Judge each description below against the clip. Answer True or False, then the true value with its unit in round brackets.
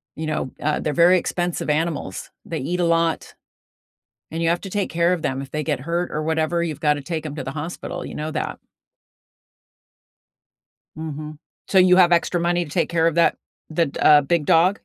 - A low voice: False (165 Hz)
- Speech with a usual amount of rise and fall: False (2.2 semitones)